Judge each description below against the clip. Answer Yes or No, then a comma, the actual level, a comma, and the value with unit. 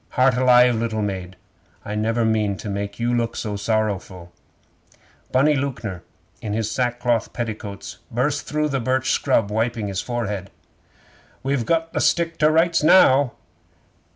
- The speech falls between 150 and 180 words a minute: No, average, 140 wpm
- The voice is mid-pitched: No, low, 115 Hz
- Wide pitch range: No, average, 4.0 semitones